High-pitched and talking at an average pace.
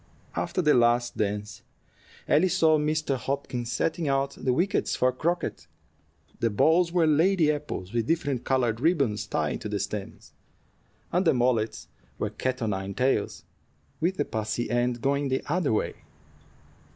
No: low, 135 Hz; average, 150 wpm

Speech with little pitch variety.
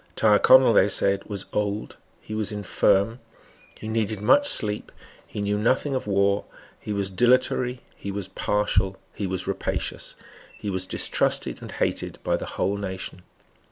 Yes: narrow, 1.9 semitones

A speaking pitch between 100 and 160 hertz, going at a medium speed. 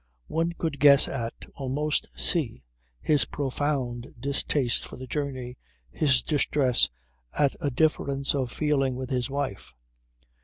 No: medium, 140 Hz; slow, 125 wpm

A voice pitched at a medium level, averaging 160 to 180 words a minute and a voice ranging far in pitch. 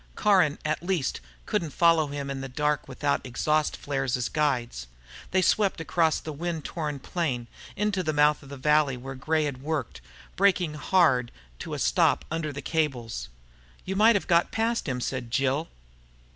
No: medium, 150 Hz; average, 170 wpm; average, 3.8 semitones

